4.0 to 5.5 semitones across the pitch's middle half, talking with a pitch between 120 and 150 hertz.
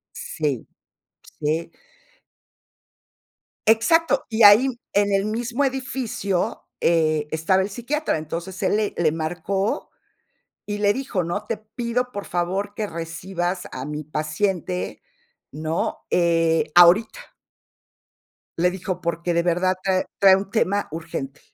No: average, 4.3 semitones; medium, 185 Hz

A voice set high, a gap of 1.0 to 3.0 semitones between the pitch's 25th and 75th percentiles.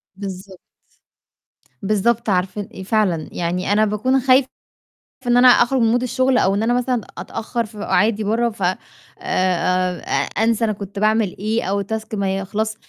No: high, 215 Hz; average, 3.4 semitones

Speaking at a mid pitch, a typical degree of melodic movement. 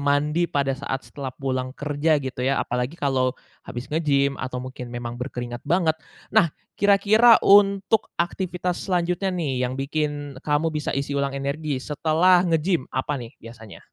Yes: medium, 145 Hz; average, 4.6 semitones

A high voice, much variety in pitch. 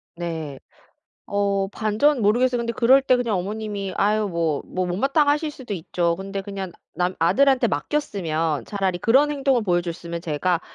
Yes: high, 200 Hz; wide, 5.8 semitones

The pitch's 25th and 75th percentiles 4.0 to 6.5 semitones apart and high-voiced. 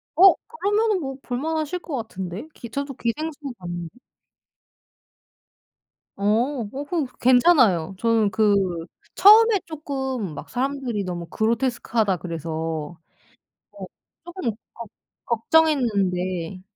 No: wide, 7.9 semitones; high, 235 Hz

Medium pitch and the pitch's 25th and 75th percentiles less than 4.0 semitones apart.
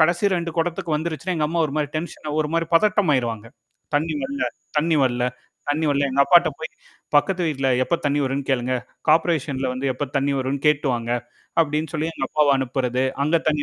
Yes: medium, 150 Hz; average, 3.4 semitones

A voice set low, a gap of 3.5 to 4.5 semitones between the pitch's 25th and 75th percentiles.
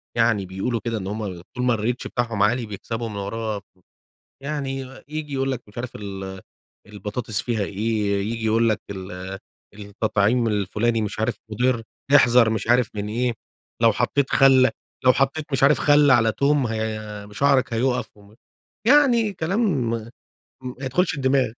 Yes: low, 115 Hz; average, 3.9 semitones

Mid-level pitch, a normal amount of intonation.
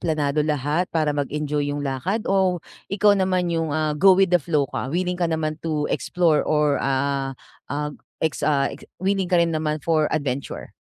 Yes: medium, 155 Hz; average, 3.4 semitones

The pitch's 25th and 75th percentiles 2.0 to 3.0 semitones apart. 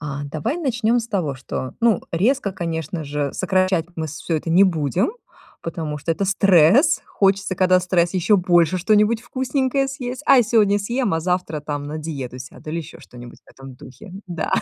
No: wide, 5.4 semitones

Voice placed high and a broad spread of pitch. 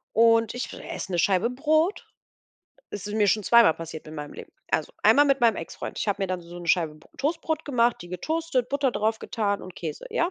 Yes: high, 220 Hz; wide, 7.2 semitones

